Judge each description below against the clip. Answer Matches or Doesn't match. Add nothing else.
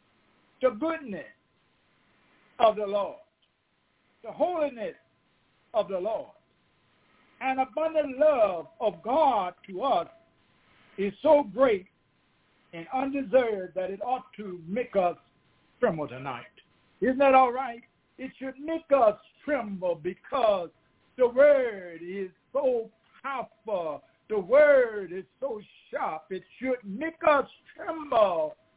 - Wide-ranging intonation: Matches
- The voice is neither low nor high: Doesn't match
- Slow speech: Matches